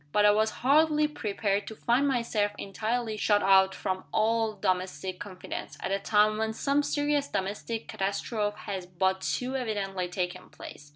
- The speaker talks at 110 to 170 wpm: Yes, average, 160 wpm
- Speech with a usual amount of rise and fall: Yes, average, 3.3 semitones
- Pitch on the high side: Yes, high, 210 Hz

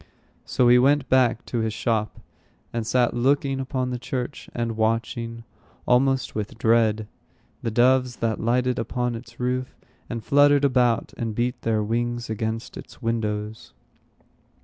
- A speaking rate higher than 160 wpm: No, average, 145 wpm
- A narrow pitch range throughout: Yes, narrow, 2.0 semitones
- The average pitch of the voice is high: No, low, 120 Hz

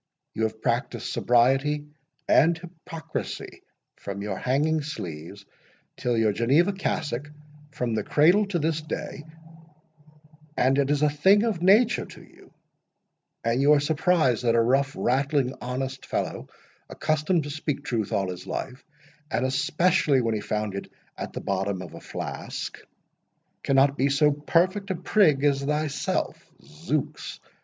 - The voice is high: No, medium, 145 Hz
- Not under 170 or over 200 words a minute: No, average, 140 wpm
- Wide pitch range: No, average, 4.2 semitones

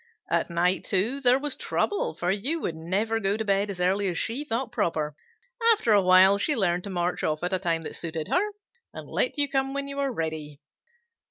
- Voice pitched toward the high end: Yes, high, 195 Hz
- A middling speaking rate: No, fast, 220 wpm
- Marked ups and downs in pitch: Yes, wide, 6.9 semitones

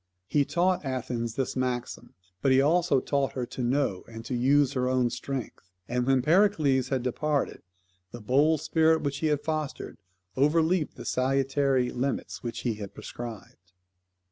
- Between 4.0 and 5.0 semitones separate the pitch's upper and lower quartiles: No, average, 3.3 semitones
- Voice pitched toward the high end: No, low, 135 Hz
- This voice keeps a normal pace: Yes, average, 160 wpm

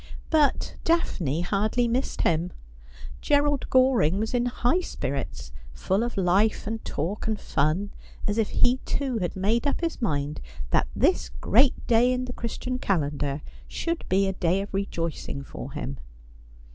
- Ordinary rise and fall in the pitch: No, wide, 7.4 semitones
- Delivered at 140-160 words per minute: Yes, average, 155 wpm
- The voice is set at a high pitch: Yes, high, 205 Hz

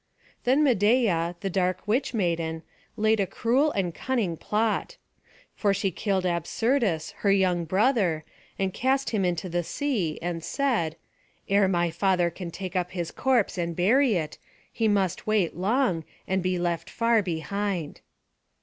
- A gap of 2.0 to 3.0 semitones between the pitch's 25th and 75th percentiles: No, average, 4.5 semitones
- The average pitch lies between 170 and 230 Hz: Yes, high, 190 Hz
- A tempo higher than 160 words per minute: No, average, 155 wpm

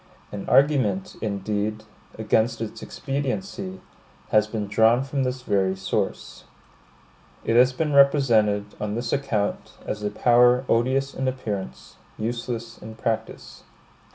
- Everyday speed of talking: No, slow, 125 wpm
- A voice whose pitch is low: Yes, low, 115 Hz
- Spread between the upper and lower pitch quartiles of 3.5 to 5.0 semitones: Yes, average, 3.9 semitones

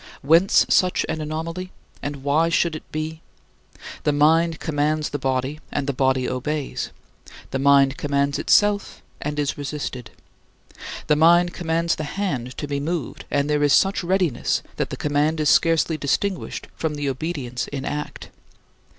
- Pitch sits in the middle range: Yes, medium, 150 Hz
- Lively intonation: No, average, 2.7 semitones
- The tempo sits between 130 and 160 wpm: Yes, average, 155 wpm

